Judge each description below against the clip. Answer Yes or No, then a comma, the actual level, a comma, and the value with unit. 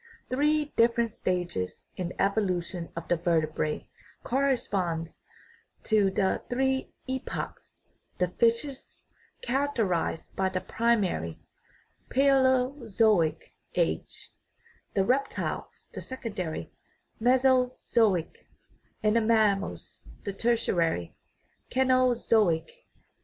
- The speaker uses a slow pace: Yes, slow, 90 wpm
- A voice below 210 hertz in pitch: No, high, 220 Hz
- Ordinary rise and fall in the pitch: No, wide, 6.1 semitones